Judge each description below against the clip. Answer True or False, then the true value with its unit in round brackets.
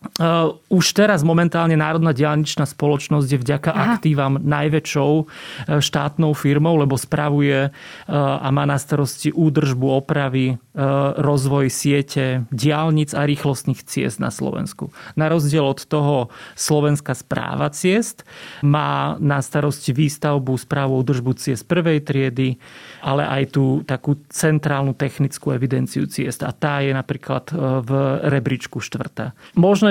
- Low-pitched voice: False (145 Hz)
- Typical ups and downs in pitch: False (2.1 semitones)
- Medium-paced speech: True (120 wpm)